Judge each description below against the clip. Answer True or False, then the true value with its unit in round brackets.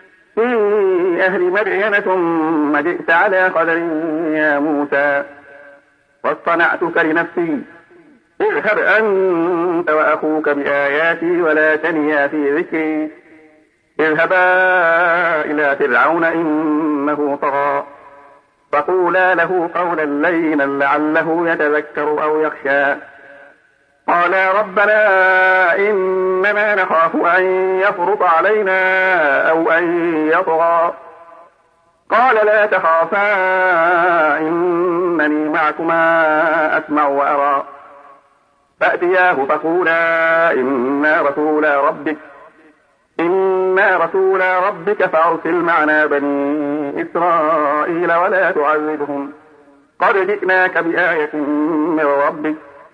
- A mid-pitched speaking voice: True (165 Hz)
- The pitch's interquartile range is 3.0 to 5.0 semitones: True (3.5 semitones)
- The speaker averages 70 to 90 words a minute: True (75 wpm)